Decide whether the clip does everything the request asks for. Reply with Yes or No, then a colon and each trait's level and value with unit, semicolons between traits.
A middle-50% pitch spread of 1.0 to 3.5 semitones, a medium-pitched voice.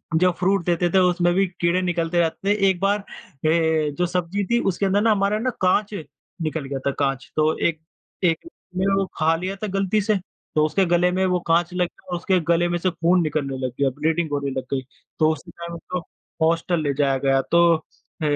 Yes: average, 3.2 semitones; medium, 175 Hz